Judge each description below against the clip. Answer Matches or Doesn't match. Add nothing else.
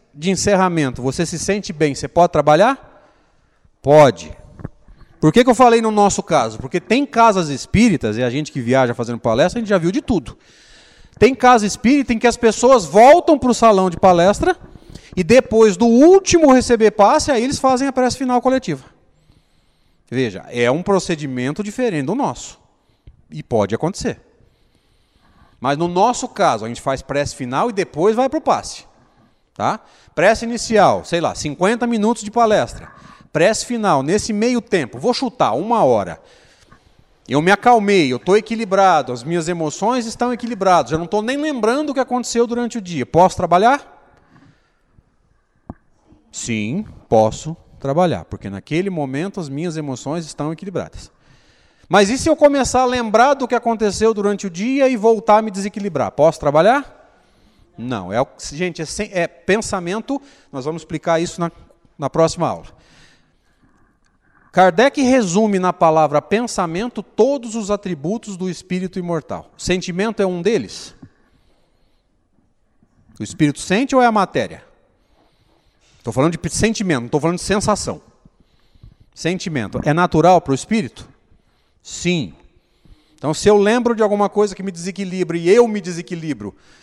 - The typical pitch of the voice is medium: Doesn't match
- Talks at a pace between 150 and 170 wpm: Matches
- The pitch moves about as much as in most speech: Doesn't match